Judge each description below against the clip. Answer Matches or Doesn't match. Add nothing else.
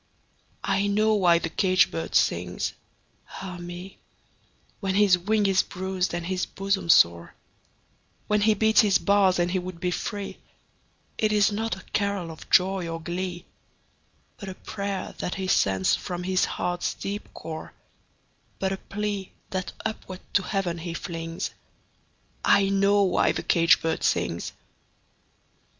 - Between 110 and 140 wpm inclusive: Doesn't match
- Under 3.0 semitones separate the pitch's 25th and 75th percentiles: Matches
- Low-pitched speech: Doesn't match